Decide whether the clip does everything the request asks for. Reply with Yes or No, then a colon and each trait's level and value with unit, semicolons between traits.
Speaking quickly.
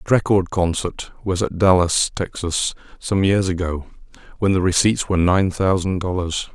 No: average, 155 wpm